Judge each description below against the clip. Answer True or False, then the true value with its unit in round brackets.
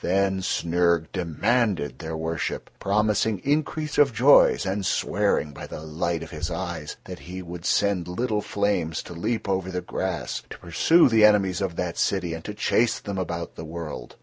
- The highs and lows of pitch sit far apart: False (3.8 semitones)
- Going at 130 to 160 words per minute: False (175 wpm)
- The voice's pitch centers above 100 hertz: False (95 Hz)